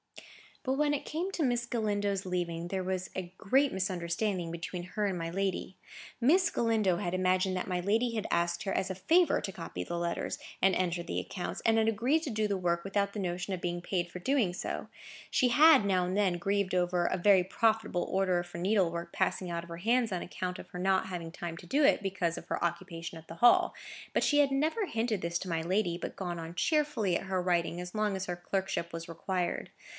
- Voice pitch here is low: No, medium, 185 Hz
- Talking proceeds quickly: Yes, fast, 225 wpm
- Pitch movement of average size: Yes, average, 3.6 semitones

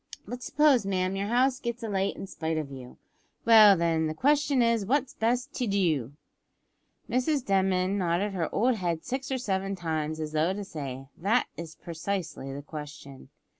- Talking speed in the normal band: Yes, average, 170 wpm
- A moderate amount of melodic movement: No, wide, 6.8 semitones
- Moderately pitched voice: No, high, 195 Hz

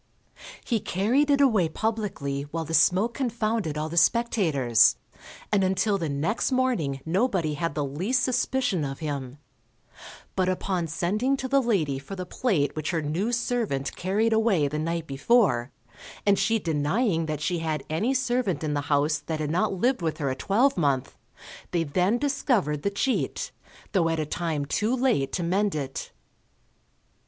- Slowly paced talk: No, average, 165 wpm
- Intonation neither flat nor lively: No, wide, 6.9 semitones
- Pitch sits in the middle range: Yes, medium, 175 Hz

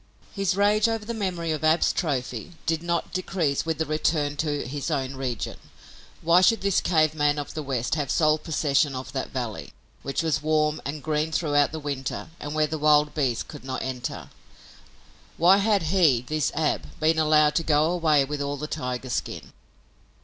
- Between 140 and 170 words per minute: No, average, 185 wpm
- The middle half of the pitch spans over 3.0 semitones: No, narrow, 2.5 semitones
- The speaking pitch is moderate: Yes, medium, 155 Hz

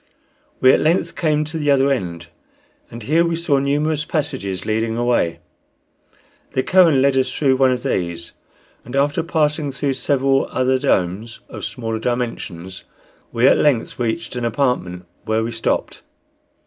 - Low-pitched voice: Yes, low, 130 Hz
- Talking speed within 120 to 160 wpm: Yes, average, 155 wpm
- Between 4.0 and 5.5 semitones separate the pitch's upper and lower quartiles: Yes, average, 4.6 semitones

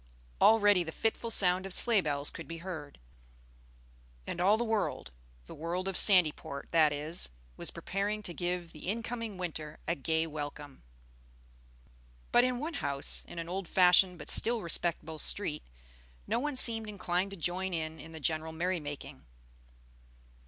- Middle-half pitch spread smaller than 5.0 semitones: Yes, average, 4.4 semitones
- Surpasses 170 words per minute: No, average, 160 wpm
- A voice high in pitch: No, medium, 175 Hz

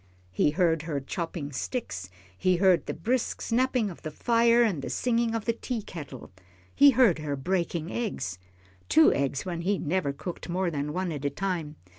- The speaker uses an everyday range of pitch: No, wide, 7.0 semitones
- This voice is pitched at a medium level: Yes, medium, 175 Hz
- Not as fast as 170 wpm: No, average, 180 wpm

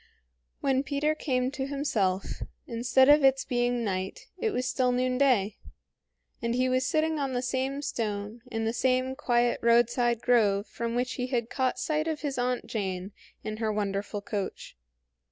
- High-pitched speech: Yes, high, 245 Hz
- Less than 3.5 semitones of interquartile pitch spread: Yes, average, 2.9 semitones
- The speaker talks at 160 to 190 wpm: Yes, average, 165 wpm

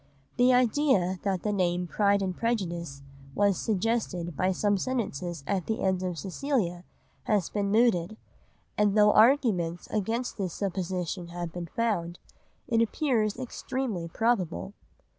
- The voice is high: Yes, high, 200 Hz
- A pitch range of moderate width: Yes, average, 4.4 semitones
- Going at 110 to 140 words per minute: Yes, slow, 135 wpm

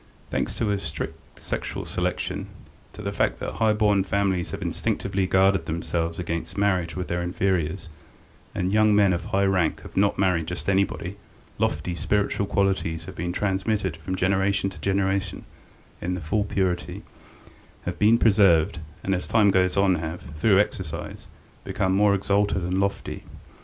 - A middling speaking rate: Yes, average, 160 wpm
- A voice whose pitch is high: No, very low, 95 Hz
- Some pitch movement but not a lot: No, narrow, 2.3 semitones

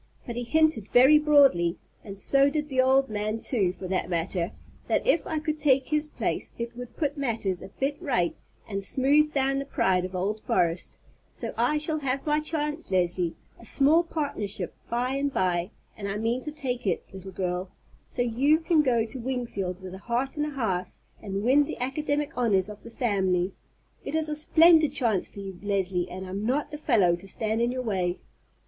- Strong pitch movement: Yes, wide, 6.9 semitones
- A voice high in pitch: Yes, high, 240 Hz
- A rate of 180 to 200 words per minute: Yes, average, 195 wpm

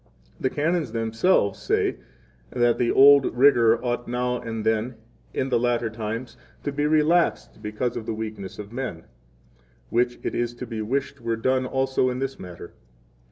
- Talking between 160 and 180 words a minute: Yes, average, 170 wpm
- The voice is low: Yes, low, 120 Hz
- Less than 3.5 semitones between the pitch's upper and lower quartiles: Yes, average, 2.9 semitones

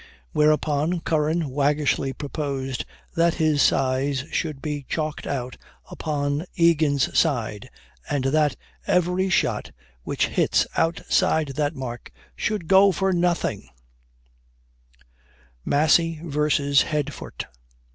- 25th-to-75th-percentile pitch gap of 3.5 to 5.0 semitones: No, average, 2.8 semitones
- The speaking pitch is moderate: Yes, medium, 150 Hz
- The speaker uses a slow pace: Yes, slow, 100 wpm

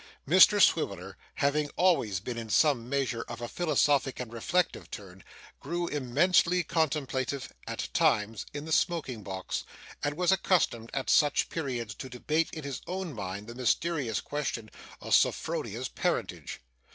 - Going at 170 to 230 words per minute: No, average, 145 wpm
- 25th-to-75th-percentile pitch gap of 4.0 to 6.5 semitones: Yes, wide, 5.5 semitones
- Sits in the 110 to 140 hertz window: Yes, low, 135 Hz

